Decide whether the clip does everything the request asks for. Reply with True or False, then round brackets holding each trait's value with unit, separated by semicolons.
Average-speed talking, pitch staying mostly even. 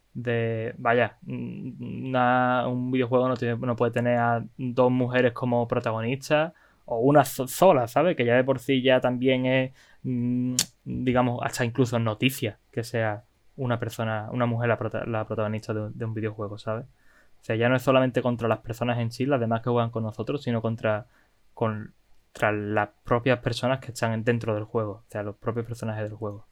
True (180 wpm; 2.2 semitones)